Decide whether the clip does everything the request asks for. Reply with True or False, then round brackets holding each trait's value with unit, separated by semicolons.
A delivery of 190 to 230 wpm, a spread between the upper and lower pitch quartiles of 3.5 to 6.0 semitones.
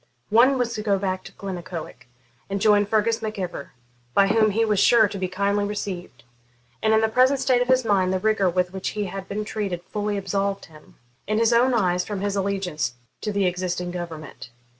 False (205 wpm; 3.0 semitones)